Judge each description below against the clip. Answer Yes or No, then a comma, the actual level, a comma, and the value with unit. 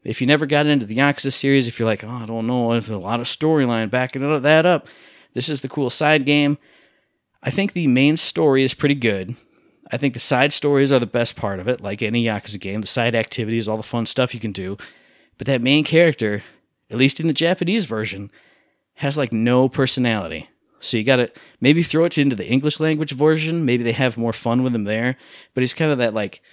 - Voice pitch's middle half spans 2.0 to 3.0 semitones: No, average, 4.2 semitones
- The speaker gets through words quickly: Yes, fast, 230 wpm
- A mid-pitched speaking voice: No, low, 130 Hz